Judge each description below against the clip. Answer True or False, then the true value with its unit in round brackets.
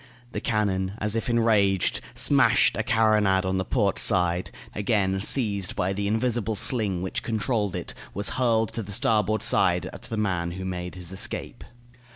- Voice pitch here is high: False (100 Hz)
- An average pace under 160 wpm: False (180 wpm)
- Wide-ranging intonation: False (2.9 semitones)